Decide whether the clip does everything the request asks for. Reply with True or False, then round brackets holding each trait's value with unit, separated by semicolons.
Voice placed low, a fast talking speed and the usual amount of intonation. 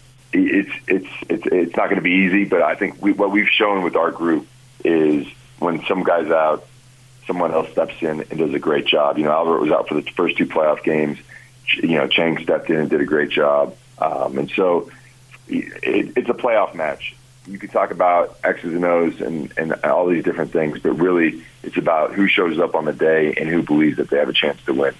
False (100 Hz; 230 wpm; 8.2 semitones)